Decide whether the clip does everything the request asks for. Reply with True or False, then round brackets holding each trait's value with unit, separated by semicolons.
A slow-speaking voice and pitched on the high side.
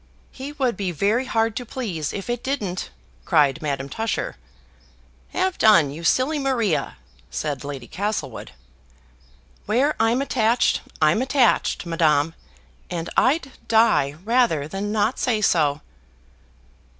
True (125 wpm; 210 Hz)